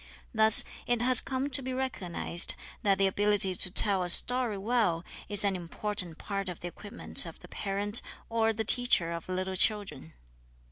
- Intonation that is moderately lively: Yes, average, 3.7 semitones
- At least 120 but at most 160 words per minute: No, average, 175 wpm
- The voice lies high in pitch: Yes, high, 205 Hz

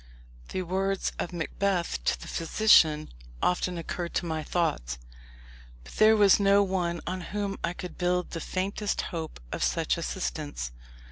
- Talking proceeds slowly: No, average, 150 wpm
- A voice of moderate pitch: Yes, medium, 180 Hz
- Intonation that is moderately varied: Yes, average, 3.2 semitones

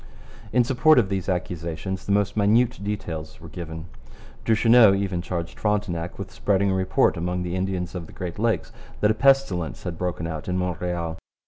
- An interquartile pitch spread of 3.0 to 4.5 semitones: Yes, average, 3.3 semitones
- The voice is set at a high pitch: No, very low, 95 Hz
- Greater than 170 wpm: Yes, average, 180 wpm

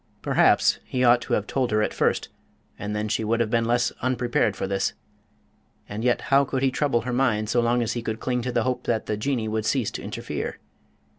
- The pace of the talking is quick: Yes, fast, 230 wpm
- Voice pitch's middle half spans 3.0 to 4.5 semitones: No, narrow, 2.6 semitones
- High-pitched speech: No, low, 120 Hz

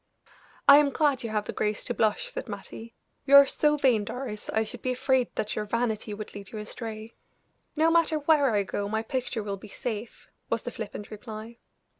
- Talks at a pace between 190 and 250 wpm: Yes, fast, 205 wpm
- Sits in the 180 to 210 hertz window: No, high, 230 Hz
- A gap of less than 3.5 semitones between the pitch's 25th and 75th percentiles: No, average, 4.3 semitones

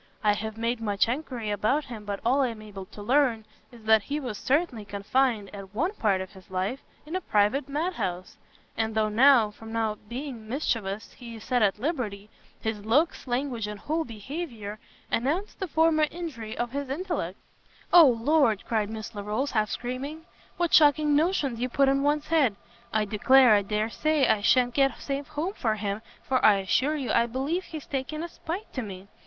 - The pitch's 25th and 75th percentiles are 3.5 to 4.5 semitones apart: No, average, 5.3 semitones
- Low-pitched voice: No, high, 240 Hz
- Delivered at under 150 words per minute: No, average, 195 wpm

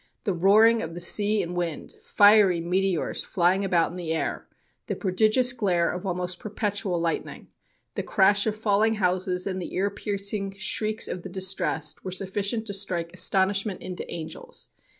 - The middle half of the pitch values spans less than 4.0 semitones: Yes, narrow, 2.5 semitones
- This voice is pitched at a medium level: No, high, 195 Hz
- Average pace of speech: Yes, average, 165 wpm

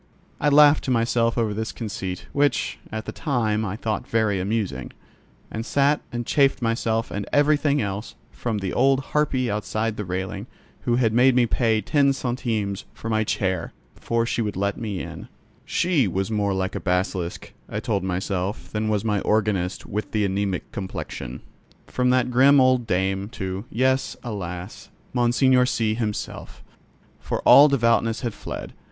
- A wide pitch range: No, average, 4.0 semitones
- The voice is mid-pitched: No, low, 110 Hz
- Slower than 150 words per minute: No, average, 165 wpm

